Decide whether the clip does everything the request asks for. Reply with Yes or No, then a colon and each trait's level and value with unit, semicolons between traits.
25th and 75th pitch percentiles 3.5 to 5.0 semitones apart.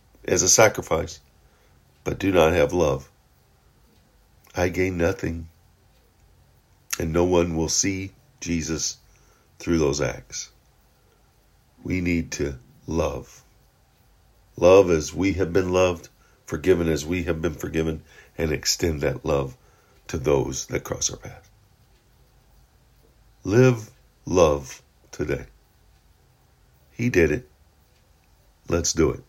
No: narrow, 2.6 semitones